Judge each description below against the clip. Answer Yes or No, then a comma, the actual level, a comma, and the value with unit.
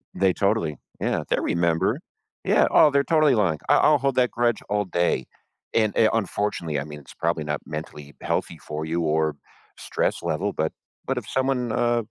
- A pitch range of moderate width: No, wide, 7.3 semitones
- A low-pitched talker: Yes, very low, 95 Hz